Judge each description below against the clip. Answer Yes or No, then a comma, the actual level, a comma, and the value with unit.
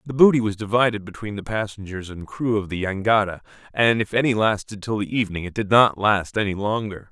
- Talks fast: Yes, fast, 210 wpm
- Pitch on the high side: No, low, 105 Hz